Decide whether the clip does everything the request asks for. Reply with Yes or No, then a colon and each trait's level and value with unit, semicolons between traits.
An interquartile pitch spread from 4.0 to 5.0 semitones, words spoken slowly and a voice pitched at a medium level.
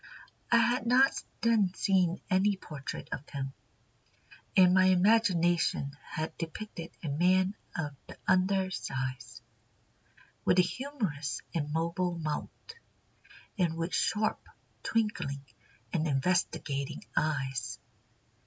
Yes: average, 4.6 semitones; slow, 105 wpm; medium, 175 Hz